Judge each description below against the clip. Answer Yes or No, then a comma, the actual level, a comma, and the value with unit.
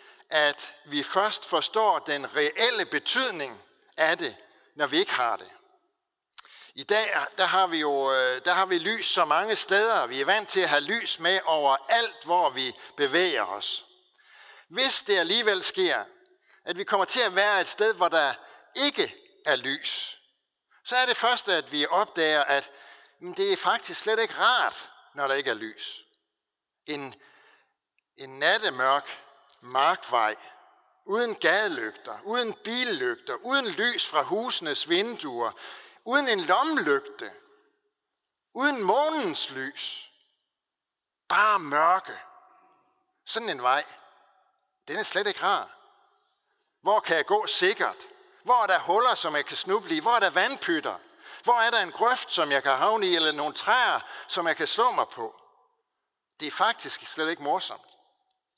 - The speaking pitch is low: No, very high, 260 Hz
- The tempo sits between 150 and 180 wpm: Yes, average, 155 wpm